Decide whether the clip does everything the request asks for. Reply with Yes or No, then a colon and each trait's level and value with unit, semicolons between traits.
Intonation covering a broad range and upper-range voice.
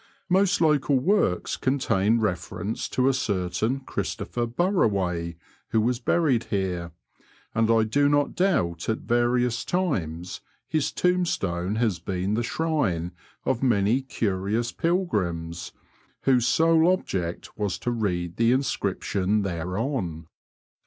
No: wide, 6.8 semitones; low, 115 Hz